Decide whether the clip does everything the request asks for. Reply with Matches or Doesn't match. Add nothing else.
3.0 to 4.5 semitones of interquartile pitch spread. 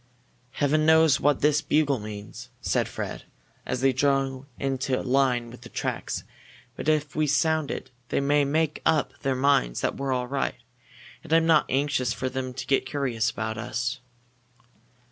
Doesn't match